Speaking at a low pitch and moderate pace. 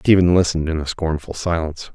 Yes: very low, 80 Hz; average, 155 wpm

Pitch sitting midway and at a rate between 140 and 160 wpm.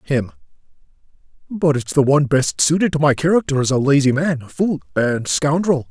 No: medium, 145 Hz; average, 175 wpm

